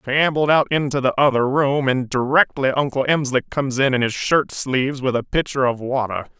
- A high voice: No, low, 135 Hz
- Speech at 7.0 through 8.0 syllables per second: No, 5.5 syllables/s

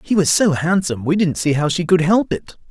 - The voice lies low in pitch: No, medium, 170 Hz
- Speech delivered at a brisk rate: Yes, fast, 265 wpm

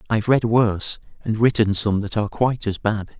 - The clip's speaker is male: Yes, male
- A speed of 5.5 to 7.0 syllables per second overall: Yes, 5.7 syllables/s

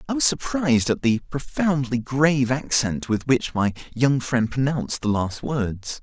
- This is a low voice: Yes, low, 130 Hz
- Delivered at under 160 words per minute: No, average, 170 wpm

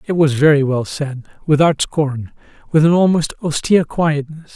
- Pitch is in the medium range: Yes, medium, 150 Hz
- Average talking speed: Yes, average, 160 wpm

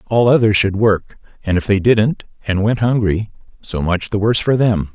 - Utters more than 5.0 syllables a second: No, 4.9 syllables/s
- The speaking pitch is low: Yes, low, 105 Hz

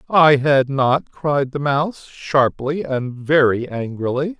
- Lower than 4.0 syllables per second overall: Yes, 3.6 syllables/s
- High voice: No, medium, 140 Hz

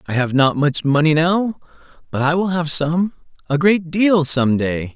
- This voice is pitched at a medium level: Yes, medium, 160 Hz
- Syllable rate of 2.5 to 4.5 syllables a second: Yes, 4.4 syllables/s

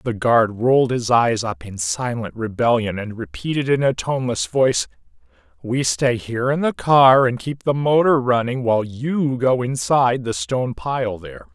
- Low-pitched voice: Yes, low, 120 Hz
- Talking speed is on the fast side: No, average, 175 wpm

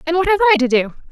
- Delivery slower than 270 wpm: No, fast, 325 wpm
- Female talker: Yes, female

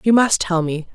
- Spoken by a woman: Yes, female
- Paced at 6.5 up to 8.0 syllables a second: No, 5.0 syllables/s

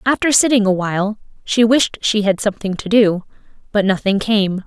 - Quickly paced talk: No, average, 180 wpm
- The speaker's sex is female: Yes, female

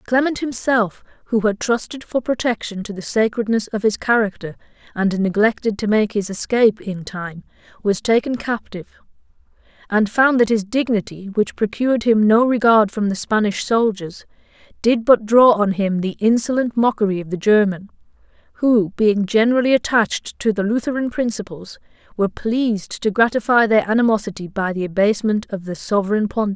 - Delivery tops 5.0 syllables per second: Yes, 5.3 syllables/s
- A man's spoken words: No, female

